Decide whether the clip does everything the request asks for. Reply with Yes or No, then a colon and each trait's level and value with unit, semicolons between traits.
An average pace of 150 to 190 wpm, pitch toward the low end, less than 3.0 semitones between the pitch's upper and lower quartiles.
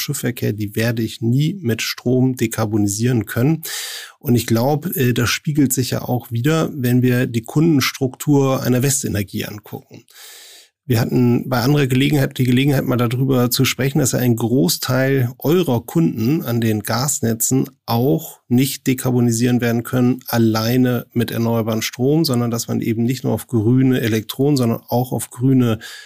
Yes: average, 155 wpm; low, 125 Hz; narrow, 2.4 semitones